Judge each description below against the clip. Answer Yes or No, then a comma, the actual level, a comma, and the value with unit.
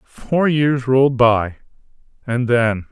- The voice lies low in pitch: Yes, low, 125 Hz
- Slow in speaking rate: Yes, slow, 105 wpm